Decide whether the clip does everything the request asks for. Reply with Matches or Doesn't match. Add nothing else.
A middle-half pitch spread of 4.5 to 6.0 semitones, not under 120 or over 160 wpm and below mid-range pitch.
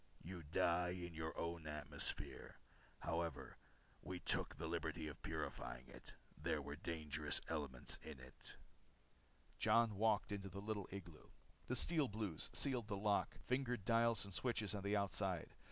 Matches